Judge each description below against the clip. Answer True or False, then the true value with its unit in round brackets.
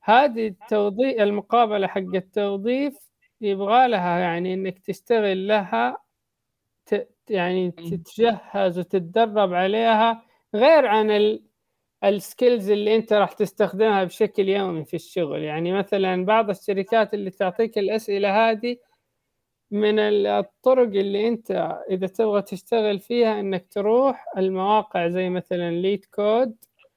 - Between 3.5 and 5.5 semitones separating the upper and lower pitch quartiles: False (3.0 semitones)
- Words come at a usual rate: True (110 wpm)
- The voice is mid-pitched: False (205 Hz)